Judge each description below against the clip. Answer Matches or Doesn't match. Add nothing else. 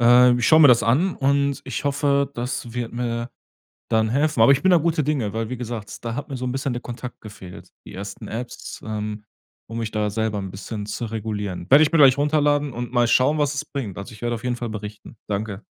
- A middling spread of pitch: Matches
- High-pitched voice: Doesn't match